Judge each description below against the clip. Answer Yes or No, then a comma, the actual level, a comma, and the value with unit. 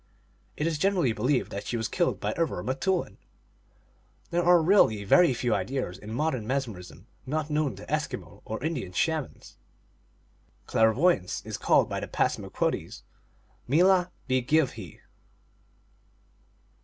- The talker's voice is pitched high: No, low, 135 Hz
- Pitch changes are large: Yes, wide, 6.9 semitones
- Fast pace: No, average, 145 wpm